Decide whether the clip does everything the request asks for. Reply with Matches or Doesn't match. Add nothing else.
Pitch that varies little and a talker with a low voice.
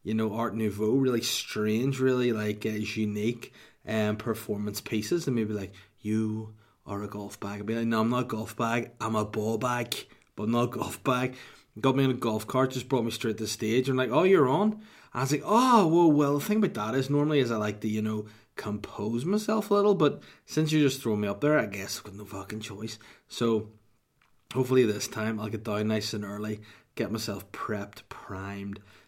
Doesn't match